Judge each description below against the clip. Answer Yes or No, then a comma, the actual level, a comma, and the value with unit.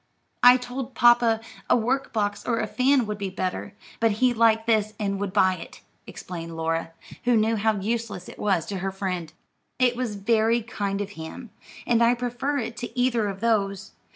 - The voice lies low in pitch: No, high, 220 Hz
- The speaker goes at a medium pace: Yes, average, 190 wpm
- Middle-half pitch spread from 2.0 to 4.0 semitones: Yes, average, 3.4 semitones